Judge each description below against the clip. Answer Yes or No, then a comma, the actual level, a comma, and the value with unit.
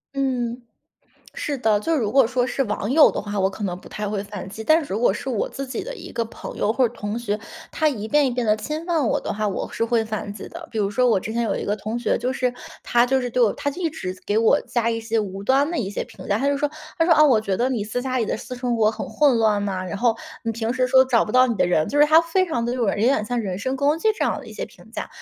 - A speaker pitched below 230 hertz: No, high, 235 Hz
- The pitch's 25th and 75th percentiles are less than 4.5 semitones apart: Yes, average, 4.1 semitones